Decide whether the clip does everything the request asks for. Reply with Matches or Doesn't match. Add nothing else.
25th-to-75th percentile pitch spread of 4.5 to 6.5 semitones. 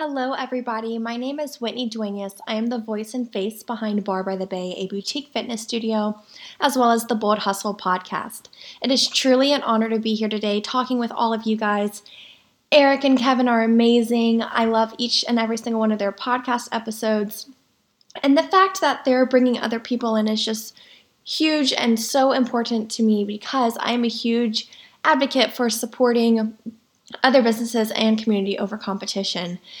Doesn't match